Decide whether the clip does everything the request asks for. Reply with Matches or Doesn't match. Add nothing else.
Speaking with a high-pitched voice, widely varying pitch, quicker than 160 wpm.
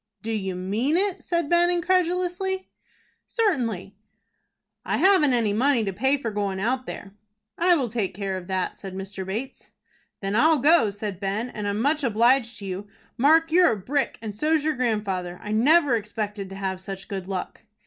Matches